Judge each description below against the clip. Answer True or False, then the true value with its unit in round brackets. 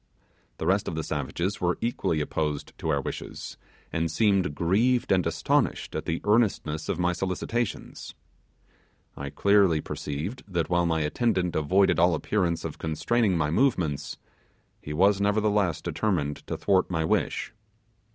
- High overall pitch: False (90 Hz)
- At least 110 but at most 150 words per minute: True (145 wpm)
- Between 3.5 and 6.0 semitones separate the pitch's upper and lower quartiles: True (4.3 semitones)